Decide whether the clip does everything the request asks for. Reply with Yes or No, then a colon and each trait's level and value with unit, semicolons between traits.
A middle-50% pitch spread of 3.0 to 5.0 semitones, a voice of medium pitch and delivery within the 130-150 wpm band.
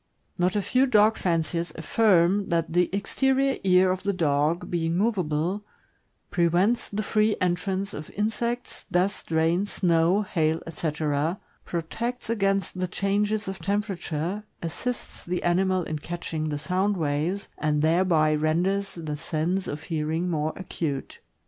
Yes: average, 3.7 semitones; medium, 180 Hz; slow, 135 wpm